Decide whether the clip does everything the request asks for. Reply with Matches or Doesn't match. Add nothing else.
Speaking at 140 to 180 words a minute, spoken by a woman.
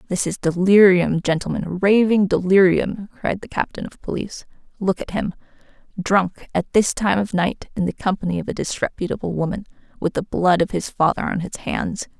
Matches